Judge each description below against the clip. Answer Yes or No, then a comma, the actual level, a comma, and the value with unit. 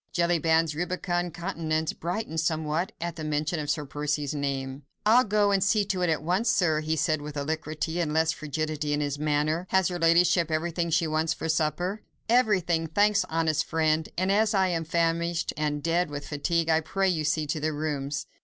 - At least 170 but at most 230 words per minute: Yes, average, 190 wpm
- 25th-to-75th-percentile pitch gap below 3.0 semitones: Yes, narrow, 2.4 semitones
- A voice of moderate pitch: Yes, medium, 160 Hz